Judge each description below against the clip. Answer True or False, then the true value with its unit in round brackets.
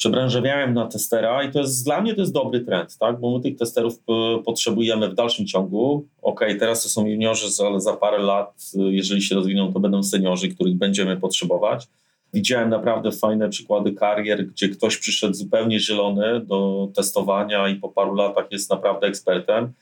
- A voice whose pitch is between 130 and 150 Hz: False (105 Hz)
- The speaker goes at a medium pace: False (180 wpm)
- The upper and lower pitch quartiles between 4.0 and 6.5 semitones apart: False (3.0 semitones)